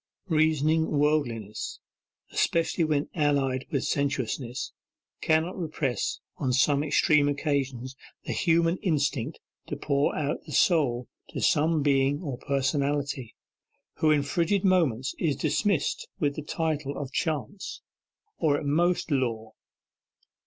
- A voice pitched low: No, medium, 145 Hz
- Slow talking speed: Yes, slow, 120 wpm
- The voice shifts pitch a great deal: No, average, 2.7 semitones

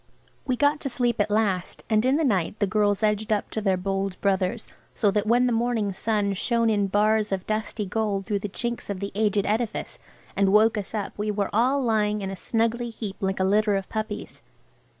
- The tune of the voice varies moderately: No, narrow, 2.2 semitones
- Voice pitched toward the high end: Yes, high, 210 Hz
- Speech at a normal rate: No, fast, 215 wpm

